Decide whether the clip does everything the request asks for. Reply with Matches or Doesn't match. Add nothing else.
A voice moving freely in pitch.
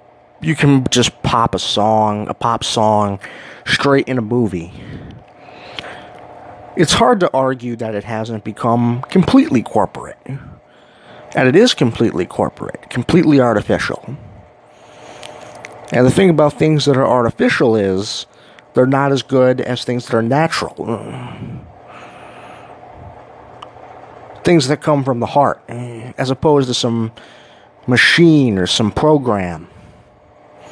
Doesn't match